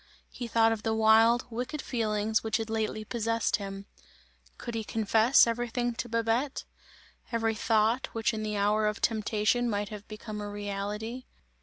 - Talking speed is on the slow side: No, average, 160 wpm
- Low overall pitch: No, high, 220 Hz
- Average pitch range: No, narrow, 1.6 semitones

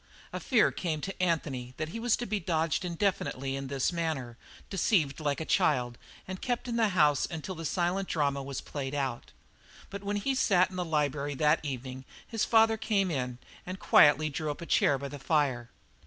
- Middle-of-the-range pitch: Yes, medium, 155 Hz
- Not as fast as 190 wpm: No, average, 200 wpm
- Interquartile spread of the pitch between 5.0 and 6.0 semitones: Yes, wide, 5.4 semitones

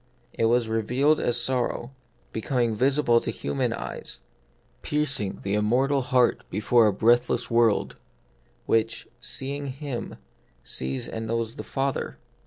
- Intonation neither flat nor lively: Yes, average, 3.1 semitones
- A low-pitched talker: Yes, low, 120 Hz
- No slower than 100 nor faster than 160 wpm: Yes, slow, 135 wpm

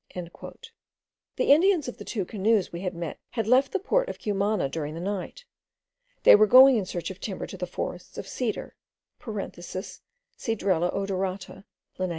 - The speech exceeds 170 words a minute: No, average, 160 wpm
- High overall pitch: Yes, high, 200 Hz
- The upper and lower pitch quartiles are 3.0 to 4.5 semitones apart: No, average, 5.2 semitones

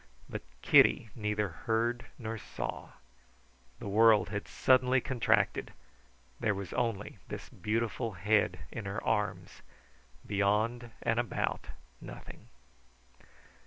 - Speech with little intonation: Yes, narrow, 2.1 semitones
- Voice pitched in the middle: No, low, 110 Hz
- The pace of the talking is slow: Yes, slow, 105 wpm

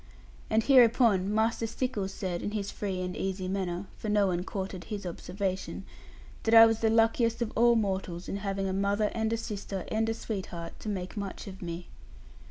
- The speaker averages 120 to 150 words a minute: No, average, 190 wpm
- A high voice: Yes, high, 200 Hz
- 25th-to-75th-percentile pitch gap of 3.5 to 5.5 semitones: No, average, 2.9 semitones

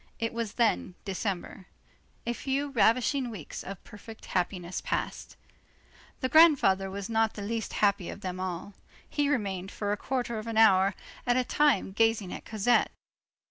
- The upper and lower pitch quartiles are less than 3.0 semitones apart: No, average, 3.8 semitones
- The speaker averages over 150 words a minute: Yes, average, 160 wpm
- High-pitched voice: Yes, high, 215 Hz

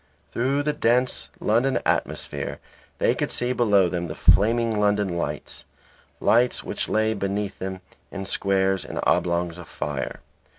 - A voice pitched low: Yes, low, 100 Hz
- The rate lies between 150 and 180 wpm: No, average, 140 wpm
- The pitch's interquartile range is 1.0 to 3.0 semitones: No, average, 4.2 semitones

